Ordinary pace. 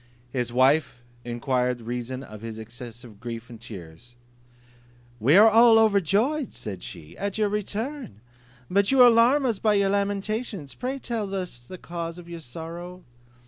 Yes: average, 150 wpm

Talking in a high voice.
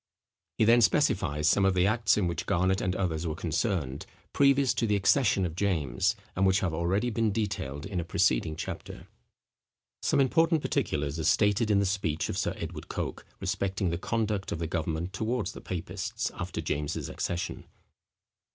No: very low, 95 Hz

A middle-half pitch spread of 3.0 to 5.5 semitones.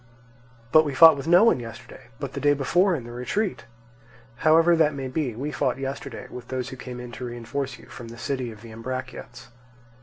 Yes: average, 3.5 semitones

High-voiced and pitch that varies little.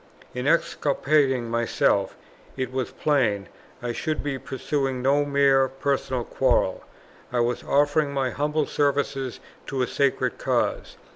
No: low, 135 Hz; narrow, 2.2 semitones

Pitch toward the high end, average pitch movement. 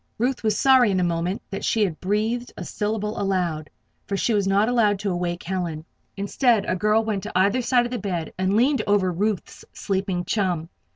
Yes: high, 200 Hz; average, 3.2 semitones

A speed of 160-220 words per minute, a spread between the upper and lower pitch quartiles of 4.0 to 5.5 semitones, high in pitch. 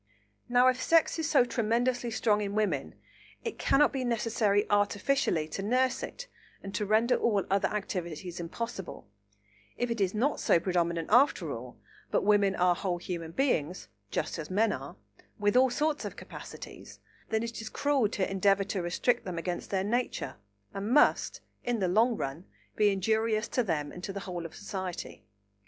Yes: average, 175 wpm; average, 4.6 semitones; high, 205 Hz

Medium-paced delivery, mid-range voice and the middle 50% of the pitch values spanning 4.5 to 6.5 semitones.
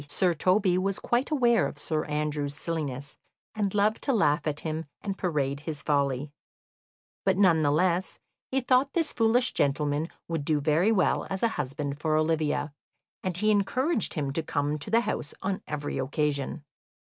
Yes: average, 170 wpm; medium, 160 Hz; average, 5.3 semitones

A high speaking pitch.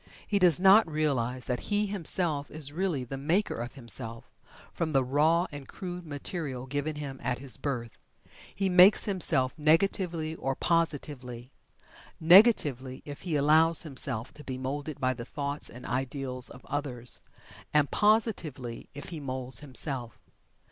No: medium, 145 Hz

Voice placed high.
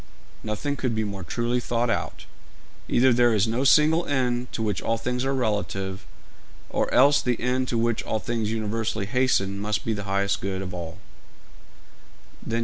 No: low, 115 Hz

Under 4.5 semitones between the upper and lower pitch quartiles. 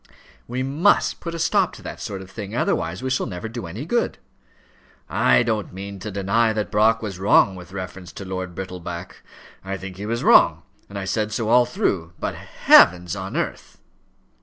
Yes: average, 4.0 semitones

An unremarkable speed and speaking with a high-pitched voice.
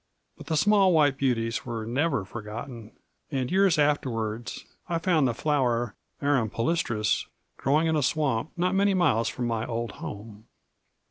No: average, 150 wpm; low, 130 Hz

